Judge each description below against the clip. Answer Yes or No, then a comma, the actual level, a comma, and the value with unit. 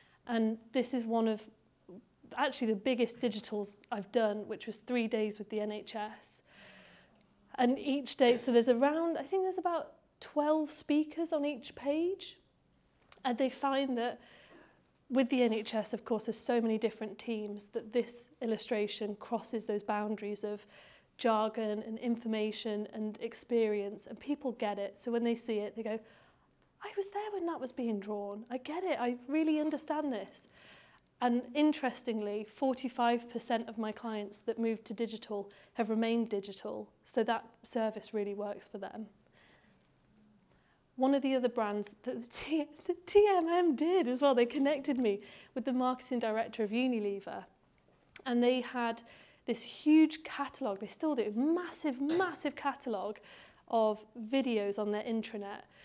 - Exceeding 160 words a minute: No, average, 155 wpm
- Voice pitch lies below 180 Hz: No, high, 235 Hz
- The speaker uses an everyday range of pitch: Yes, average, 3.9 semitones